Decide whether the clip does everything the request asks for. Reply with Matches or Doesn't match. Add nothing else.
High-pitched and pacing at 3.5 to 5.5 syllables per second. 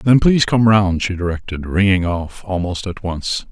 Doesn't match